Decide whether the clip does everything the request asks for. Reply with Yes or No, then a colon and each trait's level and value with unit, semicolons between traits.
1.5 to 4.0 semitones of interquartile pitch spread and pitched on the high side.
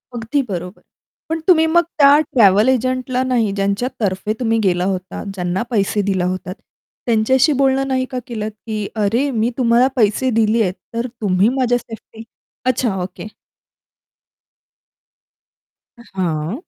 No: average, 4.6 semitones; high, 225 Hz